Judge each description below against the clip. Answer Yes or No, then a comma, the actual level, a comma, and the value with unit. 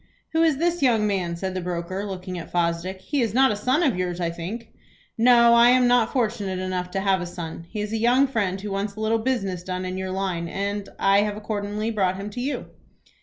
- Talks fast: Yes, fast, 235 wpm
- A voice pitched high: Yes, high, 200 Hz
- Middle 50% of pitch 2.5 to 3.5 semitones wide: No, average, 4.1 semitones